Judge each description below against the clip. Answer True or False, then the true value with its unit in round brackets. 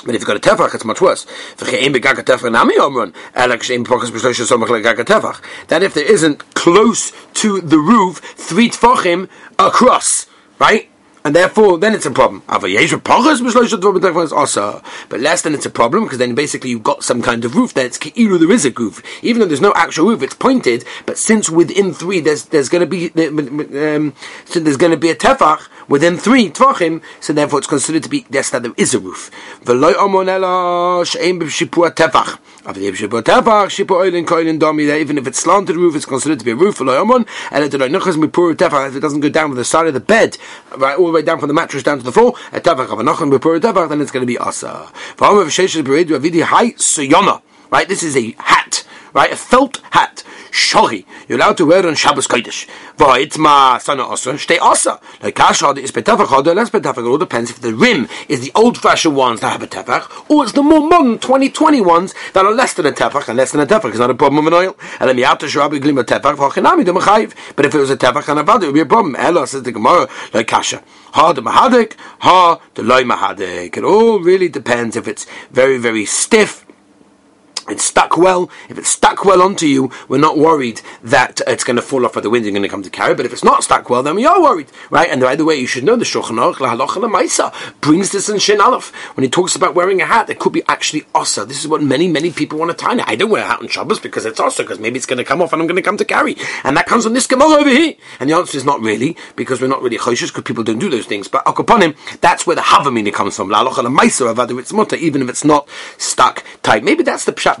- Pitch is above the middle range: False (170 Hz)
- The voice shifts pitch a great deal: True (7.1 semitones)